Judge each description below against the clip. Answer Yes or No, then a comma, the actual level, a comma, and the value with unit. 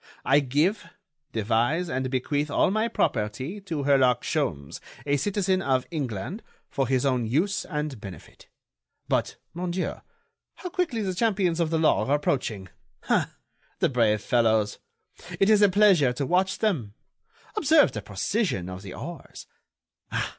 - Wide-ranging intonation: Yes, wide, 7.9 semitones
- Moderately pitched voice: Yes, medium, 145 Hz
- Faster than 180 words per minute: No, average, 145 wpm